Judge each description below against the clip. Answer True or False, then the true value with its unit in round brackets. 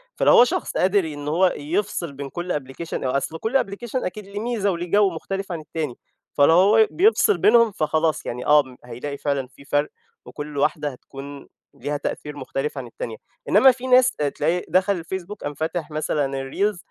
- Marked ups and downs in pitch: True (5.7 semitones)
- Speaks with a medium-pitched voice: True (160 Hz)